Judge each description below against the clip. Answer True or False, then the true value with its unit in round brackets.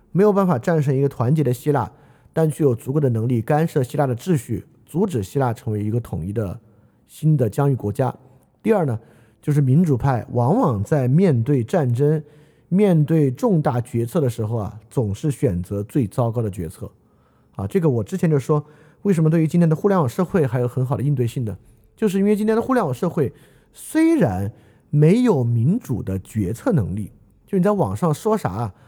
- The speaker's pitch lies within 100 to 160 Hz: True (140 Hz)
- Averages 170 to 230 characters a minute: False (295 characters per minute)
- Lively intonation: True (5.7 semitones)